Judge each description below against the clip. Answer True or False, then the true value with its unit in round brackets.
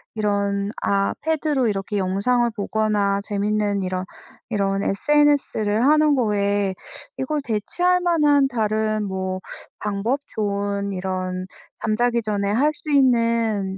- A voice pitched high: True (210 Hz)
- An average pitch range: True (3.9 semitones)